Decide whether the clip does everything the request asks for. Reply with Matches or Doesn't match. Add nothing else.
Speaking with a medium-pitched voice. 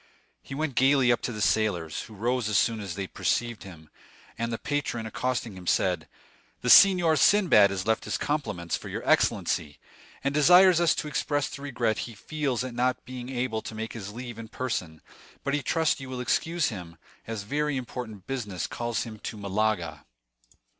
Doesn't match